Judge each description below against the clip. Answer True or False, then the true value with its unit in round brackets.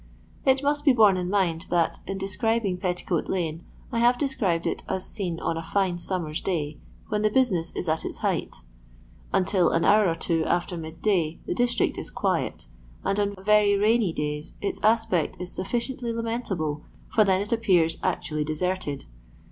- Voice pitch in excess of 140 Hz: True (190 Hz)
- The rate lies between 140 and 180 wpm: True (170 wpm)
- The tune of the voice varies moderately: True (4.5 semitones)